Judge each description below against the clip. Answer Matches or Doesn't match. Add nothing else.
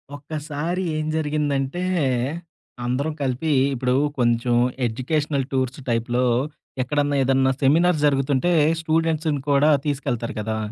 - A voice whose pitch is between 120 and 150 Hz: Matches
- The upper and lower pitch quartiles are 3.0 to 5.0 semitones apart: Matches